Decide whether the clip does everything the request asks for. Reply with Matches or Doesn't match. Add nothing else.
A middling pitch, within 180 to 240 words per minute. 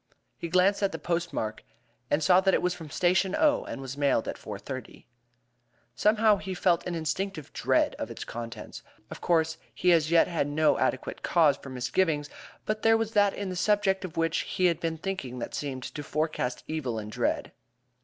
Matches